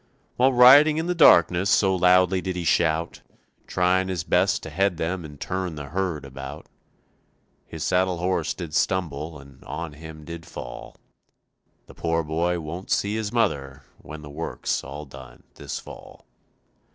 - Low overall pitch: Yes, very low, 85 Hz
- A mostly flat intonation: No, average, 3.6 semitones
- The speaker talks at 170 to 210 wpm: No, average, 160 wpm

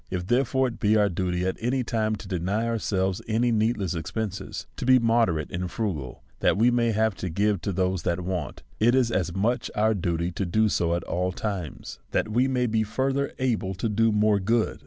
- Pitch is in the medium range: No, low, 105 Hz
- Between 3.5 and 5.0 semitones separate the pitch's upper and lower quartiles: Yes, average, 4.0 semitones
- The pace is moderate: No, fast, 220 wpm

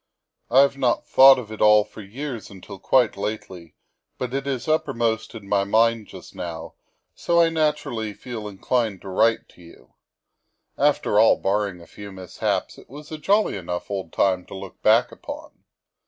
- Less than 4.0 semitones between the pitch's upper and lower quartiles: No, average, 5.3 semitones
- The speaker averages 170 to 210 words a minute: Yes, average, 175 wpm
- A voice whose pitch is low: Yes, low, 110 Hz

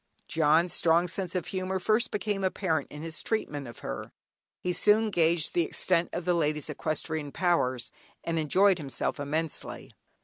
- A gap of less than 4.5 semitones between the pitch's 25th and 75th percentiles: Yes, average, 3.5 semitones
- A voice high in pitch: No, medium, 170 Hz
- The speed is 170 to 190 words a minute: No, average, 160 wpm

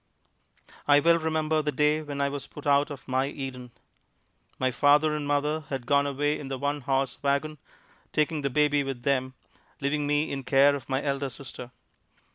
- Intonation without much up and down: Yes, narrow, 1.6 semitones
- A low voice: No, medium, 145 Hz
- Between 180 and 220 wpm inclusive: Yes, average, 185 wpm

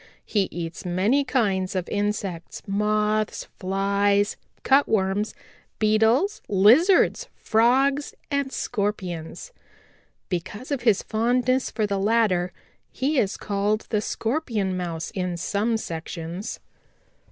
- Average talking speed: No, slow, 105 wpm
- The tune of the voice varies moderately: Yes, average, 3.9 semitones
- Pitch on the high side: Yes, high, 210 Hz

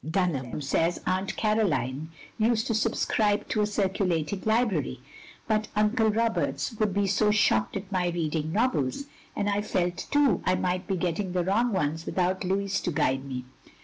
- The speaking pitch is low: No, high, 190 Hz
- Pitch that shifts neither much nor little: Yes, average, 4.0 semitones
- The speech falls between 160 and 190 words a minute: Yes, average, 165 wpm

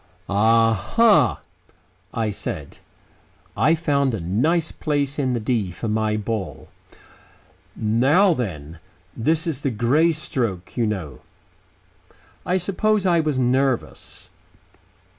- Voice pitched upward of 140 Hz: No, low, 125 Hz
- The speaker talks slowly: Yes, slow, 115 wpm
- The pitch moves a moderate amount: No, wide, 6.6 semitones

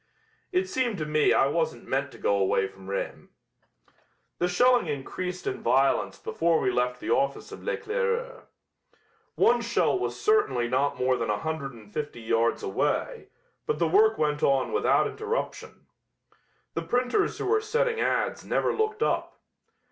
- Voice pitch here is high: No, medium, 165 Hz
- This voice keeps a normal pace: Yes, average, 160 wpm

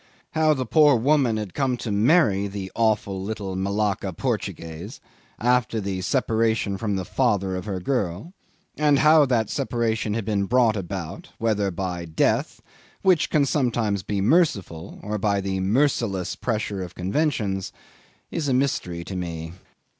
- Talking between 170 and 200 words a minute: No, average, 150 wpm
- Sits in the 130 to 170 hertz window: No, low, 105 Hz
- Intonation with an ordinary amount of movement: Yes, average, 4.7 semitones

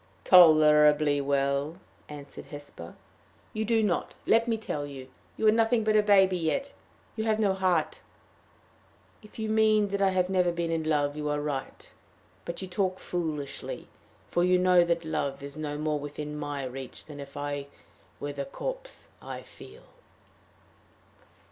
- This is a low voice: No, medium, 160 Hz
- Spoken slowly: No, average, 160 wpm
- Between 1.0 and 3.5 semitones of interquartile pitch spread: No, average, 5.3 semitones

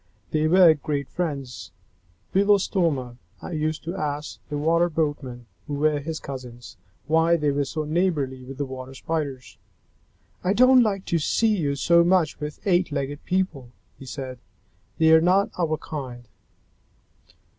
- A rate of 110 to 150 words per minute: Yes, average, 145 wpm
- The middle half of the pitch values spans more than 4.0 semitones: No, average, 3.7 semitones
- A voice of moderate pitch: Yes, medium, 155 Hz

